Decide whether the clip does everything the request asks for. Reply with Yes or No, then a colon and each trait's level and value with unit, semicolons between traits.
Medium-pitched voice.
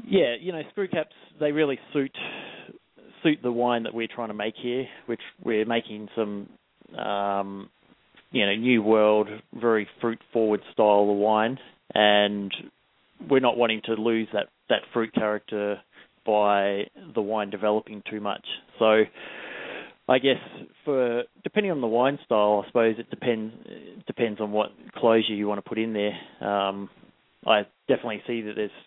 No: low, 110 Hz